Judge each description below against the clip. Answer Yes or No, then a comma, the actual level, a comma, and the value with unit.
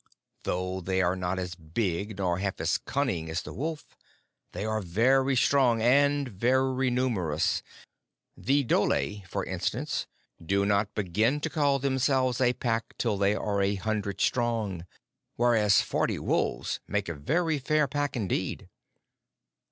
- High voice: No, low, 110 Hz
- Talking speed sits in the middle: Yes, average, 145 wpm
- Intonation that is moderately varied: No, wide, 5.8 semitones